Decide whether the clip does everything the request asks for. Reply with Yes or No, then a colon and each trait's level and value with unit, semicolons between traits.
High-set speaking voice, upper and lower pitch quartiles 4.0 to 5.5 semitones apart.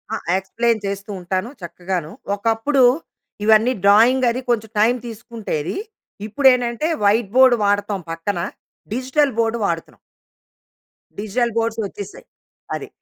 No: high, 220 Hz; average, 3.3 semitones